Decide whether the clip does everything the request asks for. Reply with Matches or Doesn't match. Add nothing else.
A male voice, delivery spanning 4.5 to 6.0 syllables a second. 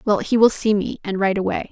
Doesn't match